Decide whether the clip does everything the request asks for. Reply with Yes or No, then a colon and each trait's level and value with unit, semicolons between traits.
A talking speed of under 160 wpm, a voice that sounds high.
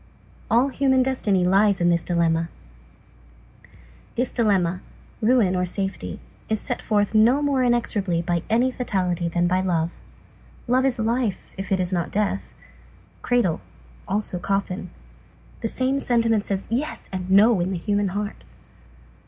Yes: average, 145 wpm; high, 200 Hz